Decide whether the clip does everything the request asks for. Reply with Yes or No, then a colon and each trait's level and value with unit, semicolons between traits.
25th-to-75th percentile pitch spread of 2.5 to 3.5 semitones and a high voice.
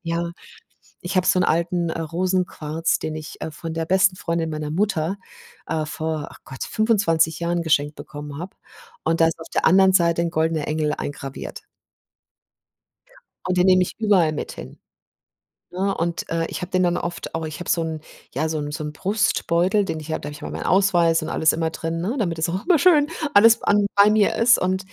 No: average, 2.9 semitones; medium, 170 Hz